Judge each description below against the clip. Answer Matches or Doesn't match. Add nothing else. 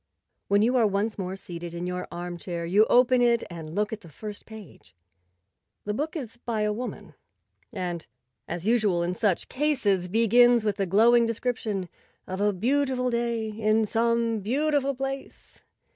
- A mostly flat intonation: Doesn't match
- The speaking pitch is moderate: Doesn't match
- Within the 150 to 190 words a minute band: Matches